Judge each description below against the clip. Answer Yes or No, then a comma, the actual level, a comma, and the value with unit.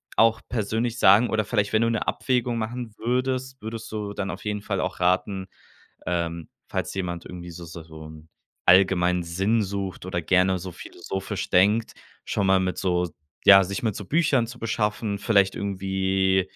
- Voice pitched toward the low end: Yes, low, 100 Hz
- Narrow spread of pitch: No, average, 3.4 semitones